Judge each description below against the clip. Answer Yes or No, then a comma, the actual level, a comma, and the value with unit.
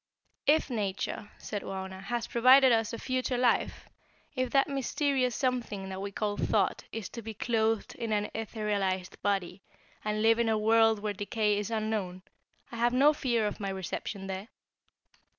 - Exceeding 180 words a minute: No, average, 170 wpm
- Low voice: No, high, 220 Hz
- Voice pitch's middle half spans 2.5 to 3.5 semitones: Yes, average, 3.0 semitones